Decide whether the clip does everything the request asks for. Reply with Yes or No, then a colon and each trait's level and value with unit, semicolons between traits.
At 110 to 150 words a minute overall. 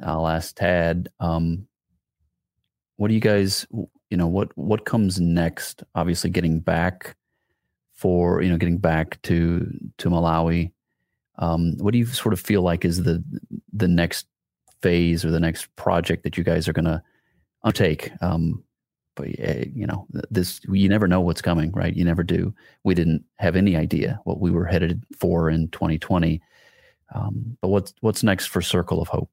No: average, 170 wpm